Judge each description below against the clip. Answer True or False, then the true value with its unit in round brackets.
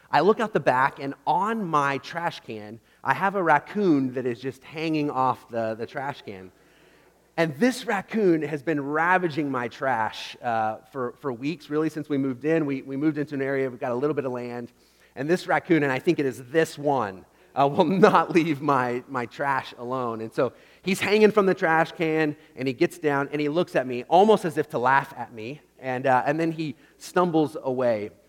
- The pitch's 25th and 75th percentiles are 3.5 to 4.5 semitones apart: True (4.1 semitones)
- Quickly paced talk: True (215 wpm)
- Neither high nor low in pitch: True (145 Hz)